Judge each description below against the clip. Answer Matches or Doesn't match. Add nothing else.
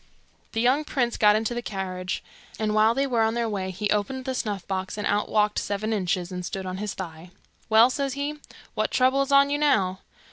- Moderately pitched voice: Doesn't match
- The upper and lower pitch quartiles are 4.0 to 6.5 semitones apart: Matches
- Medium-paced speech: Doesn't match